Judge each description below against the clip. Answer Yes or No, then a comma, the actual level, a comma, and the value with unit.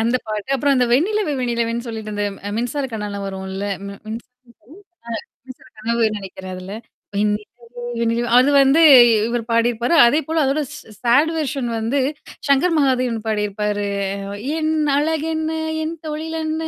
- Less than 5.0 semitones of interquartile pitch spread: No, average, 5.3 semitones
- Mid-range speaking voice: No, high, 240 Hz